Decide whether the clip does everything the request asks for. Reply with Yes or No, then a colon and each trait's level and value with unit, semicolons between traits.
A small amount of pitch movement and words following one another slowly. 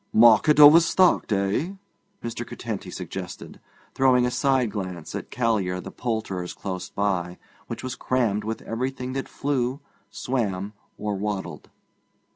No: average, 4.8 semitones; slow, 125 wpm